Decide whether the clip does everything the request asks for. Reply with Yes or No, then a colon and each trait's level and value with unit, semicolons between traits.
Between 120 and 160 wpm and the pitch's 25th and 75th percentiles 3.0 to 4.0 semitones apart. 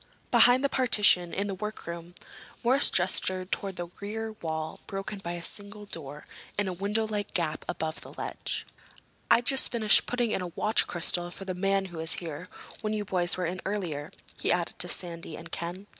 No: average, 185 wpm; average, 3.5 semitones